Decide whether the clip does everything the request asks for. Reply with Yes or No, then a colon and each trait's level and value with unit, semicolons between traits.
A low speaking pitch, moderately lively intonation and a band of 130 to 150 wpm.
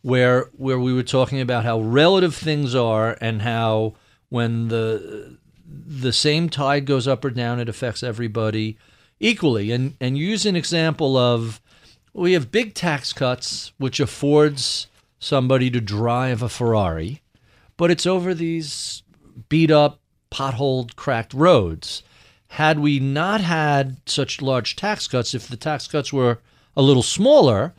Yes: low, 130 Hz; average, 4.2 semitones; average, 145 wpm